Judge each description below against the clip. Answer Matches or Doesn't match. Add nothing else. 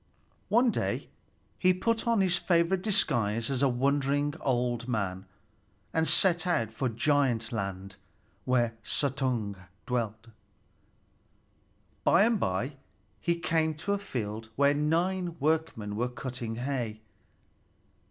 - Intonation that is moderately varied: Doesn't match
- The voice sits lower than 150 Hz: Matches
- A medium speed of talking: Doesn't match